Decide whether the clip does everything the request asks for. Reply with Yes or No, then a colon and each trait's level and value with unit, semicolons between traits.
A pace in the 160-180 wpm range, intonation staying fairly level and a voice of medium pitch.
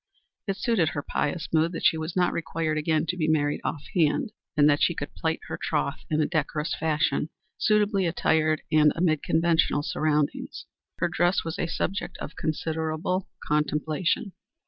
Yes: average, 170 wpm; narrow, 2.2 semitones; medium, 160 Hz